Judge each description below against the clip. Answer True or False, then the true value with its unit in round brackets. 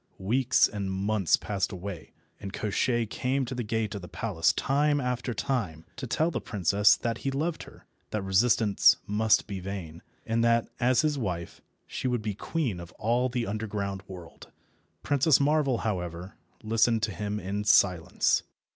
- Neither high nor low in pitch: False (110 Hz)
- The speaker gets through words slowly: False (165 wpm)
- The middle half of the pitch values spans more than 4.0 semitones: True (4.4 semitones)